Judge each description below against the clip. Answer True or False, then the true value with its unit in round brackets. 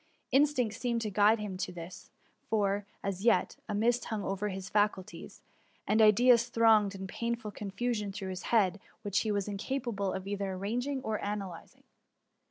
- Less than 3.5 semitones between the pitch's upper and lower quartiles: True (2.9 semitones)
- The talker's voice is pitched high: True (210 Hz)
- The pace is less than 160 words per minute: False (170 wpm)